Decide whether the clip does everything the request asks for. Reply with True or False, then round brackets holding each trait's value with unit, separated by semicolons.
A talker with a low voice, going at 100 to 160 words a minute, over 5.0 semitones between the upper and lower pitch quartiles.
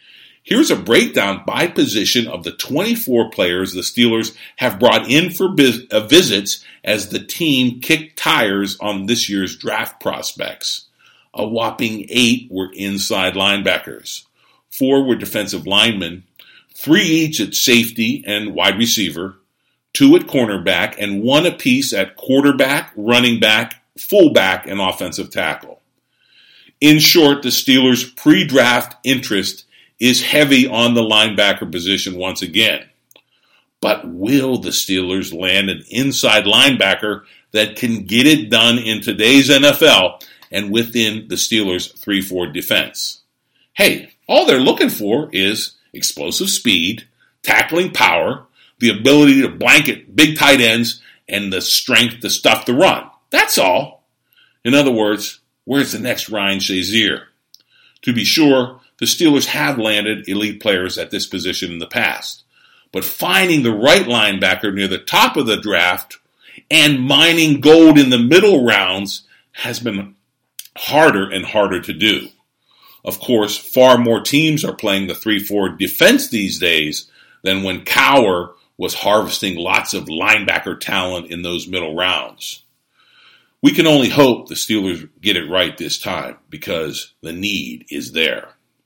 True (115 Hz; 140 wpm; 5.5 semitones)